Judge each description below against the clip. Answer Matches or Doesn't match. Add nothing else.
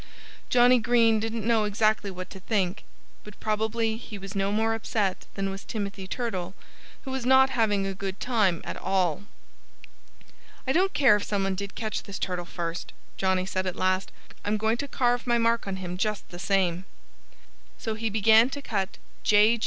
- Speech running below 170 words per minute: Doesn't match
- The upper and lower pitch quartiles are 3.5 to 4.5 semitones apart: Doesn't match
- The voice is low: Doesn't match